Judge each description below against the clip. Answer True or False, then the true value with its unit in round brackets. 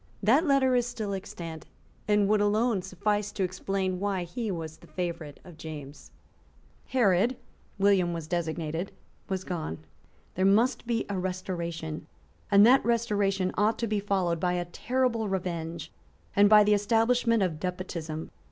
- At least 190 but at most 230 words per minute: False (150 wpm)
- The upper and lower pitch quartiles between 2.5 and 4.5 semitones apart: True (3.7 semitones)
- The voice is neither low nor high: False (195 Hz)